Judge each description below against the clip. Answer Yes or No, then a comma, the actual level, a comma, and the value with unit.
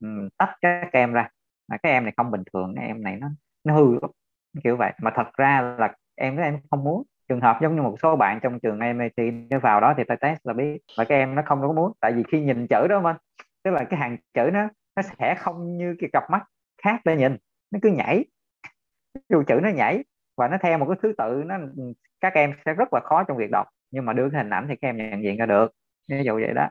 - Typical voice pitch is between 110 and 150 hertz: Yes, medium, 140 Hz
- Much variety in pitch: Yes, wide, 5.7 semitones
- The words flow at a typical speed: No, fast, 265 wpm